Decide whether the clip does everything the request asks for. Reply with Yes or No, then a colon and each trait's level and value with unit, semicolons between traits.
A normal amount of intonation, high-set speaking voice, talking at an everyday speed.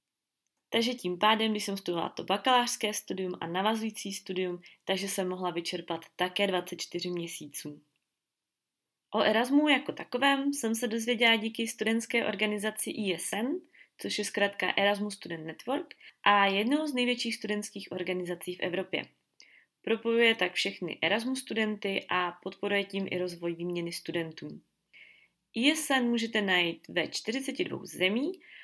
Yes: average, 4.3 semitones; high, 205 Hz; average, 130 wpm